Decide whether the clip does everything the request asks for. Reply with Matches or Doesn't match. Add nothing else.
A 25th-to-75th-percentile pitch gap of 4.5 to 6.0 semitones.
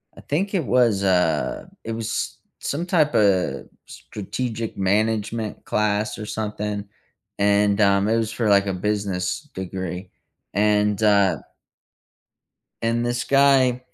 Doesn't match